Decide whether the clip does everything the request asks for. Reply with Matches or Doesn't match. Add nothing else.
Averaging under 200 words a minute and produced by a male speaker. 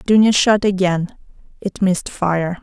Doesn't match